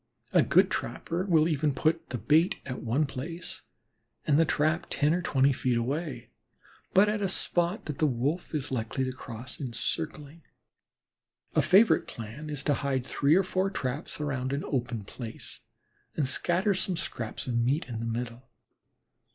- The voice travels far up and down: No, average, 4.6 semitones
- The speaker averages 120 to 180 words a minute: Yes, average, 170 wpm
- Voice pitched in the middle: Yes, medium, 145 Hz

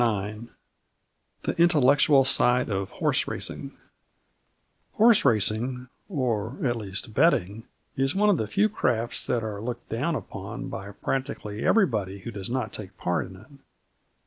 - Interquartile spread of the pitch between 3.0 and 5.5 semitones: Yes, average, 4.4 semitones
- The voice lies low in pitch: Yes, low, 120 Hz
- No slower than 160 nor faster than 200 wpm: No, average, 145 wpm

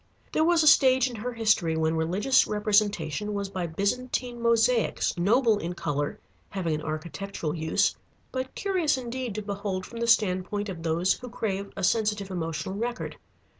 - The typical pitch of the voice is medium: No, high, 205 Hz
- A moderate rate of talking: Yes, average, 165 wpm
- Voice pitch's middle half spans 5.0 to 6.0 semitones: Yes, average, 5.3 semitones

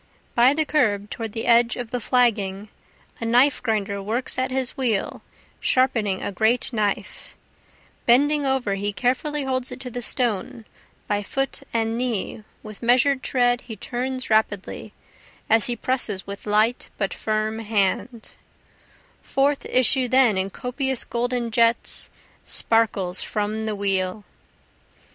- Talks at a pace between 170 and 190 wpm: No, average, 140 wpm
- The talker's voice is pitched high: Yes, high, 235 Hz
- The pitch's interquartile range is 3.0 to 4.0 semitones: Yes, average, 3.5 semitones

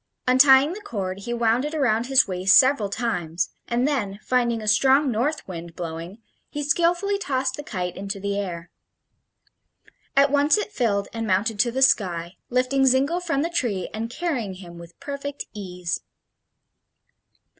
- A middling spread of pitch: No, wide, 6.3 semitones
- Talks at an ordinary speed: Yes, average, 160 wpm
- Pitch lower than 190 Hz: No, high, 235 Hz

